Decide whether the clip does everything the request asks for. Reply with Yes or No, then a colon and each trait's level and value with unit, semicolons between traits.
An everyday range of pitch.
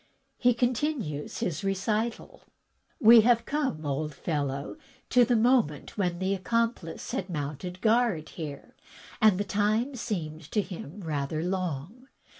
No: wide, 6.9 semitones